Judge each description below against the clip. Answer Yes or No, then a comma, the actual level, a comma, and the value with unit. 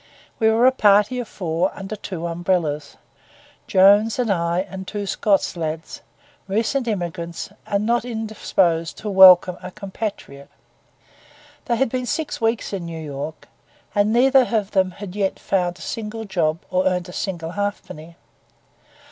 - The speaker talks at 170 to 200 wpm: No, average, 150 wpm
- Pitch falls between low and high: No, high, 195 Hz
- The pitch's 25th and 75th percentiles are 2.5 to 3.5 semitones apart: No, average, 4.1 semitones